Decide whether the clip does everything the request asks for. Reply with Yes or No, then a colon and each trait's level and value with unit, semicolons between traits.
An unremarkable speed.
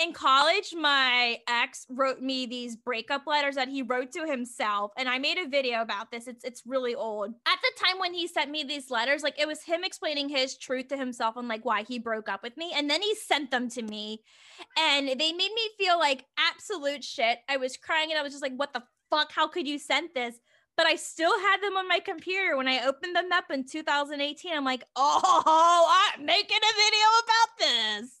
No: fast, 225 wpm